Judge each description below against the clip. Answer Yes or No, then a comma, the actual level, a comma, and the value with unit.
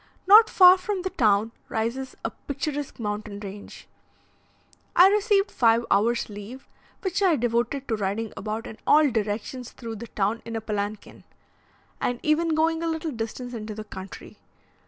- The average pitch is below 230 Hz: No, high, 235 Hz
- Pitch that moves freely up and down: Yes, wide, 6.7 semitones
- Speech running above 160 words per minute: No, average, 155 wpm